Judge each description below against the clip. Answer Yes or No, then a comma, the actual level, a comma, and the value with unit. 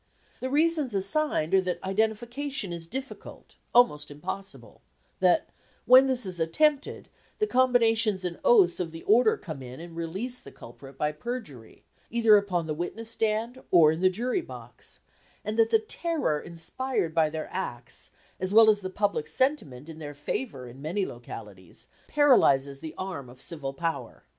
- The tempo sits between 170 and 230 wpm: No, average, 160 wpm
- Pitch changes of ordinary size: No, wide, 7.6 semitones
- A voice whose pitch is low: No, high, 190 Hz